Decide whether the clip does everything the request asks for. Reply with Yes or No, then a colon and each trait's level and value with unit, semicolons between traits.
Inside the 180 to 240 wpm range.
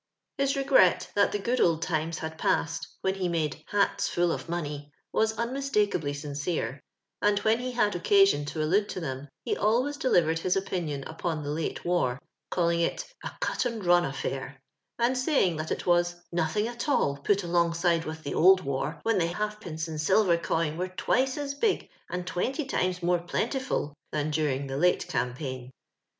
Yes: average, 185 wpm